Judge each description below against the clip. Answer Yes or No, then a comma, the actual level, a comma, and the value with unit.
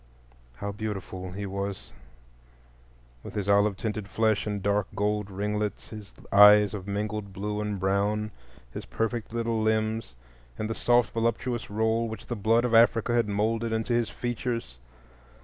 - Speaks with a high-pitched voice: No, low, 105 Hz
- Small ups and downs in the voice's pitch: Yes, narrow, 1.9 semitones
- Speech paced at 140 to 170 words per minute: Yes, average, 150 wpm